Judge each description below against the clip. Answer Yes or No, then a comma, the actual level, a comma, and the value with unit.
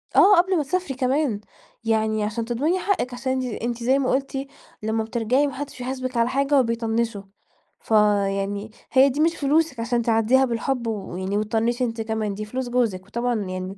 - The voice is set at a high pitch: Yes, high, 235 Hz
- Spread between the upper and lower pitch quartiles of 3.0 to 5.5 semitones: Yes, average, 3.4 semitones